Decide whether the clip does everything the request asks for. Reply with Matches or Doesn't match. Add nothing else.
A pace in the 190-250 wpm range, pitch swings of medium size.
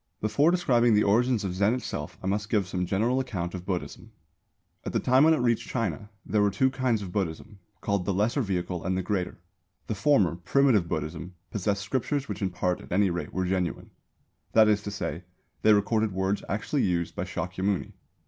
Matches